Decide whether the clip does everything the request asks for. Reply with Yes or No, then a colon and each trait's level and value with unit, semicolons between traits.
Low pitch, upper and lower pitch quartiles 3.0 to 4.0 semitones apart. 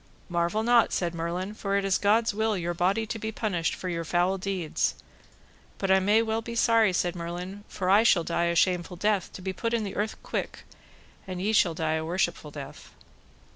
No: high, 190 Hz; average, 3.7 semitones